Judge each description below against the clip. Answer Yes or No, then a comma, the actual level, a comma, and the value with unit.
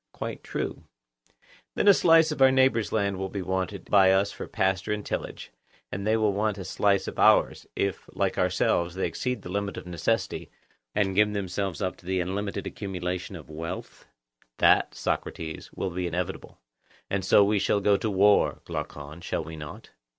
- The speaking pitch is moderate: No, very low, 95 Hz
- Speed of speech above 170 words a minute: Yes, average, 180 wpm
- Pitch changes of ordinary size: No, narrow, 2.3 semitones